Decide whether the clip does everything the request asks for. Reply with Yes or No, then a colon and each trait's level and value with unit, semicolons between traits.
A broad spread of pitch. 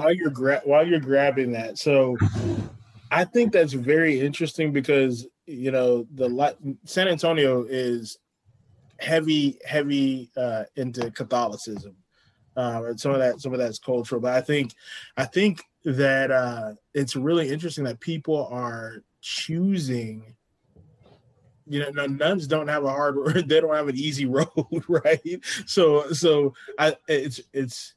No: average, 3.7 semitones